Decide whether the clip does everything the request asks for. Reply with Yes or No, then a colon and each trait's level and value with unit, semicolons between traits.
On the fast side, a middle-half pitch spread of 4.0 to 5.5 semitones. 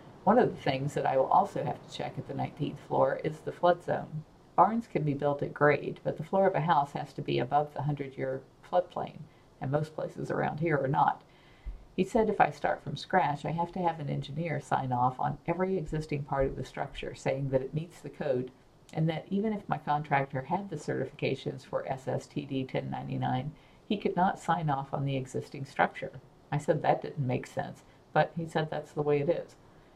No: fast, 215 wpm; average, 3.5 semitones